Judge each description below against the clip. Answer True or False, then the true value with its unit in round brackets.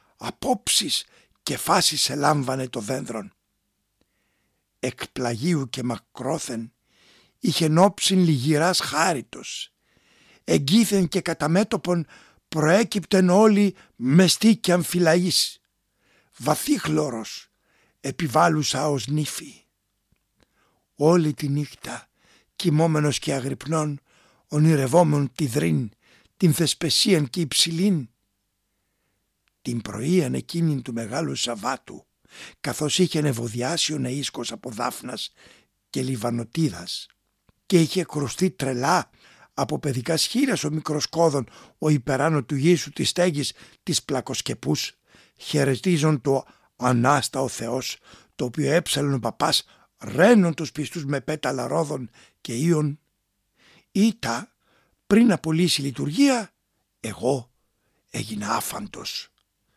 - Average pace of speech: False (100 wpm)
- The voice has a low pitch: False (150 Hz)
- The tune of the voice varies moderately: True (4.7 semitones)